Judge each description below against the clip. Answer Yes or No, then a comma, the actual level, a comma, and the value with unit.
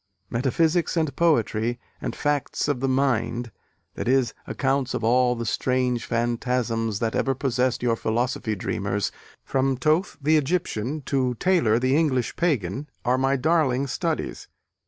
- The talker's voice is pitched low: Yes, low, 130 Hz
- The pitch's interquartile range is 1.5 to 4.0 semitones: Yes, average, 3.1 semitones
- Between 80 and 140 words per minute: Yes, slow, 135 wpm